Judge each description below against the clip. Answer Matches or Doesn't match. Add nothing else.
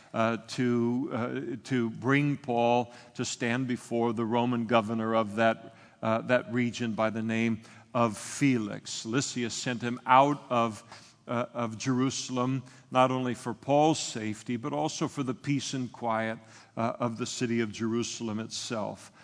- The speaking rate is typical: Matches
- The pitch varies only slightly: Matches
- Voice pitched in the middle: Doesn't match